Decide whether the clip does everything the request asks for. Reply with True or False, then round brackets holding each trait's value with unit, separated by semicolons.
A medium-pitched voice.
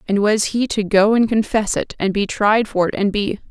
False (210 Hz)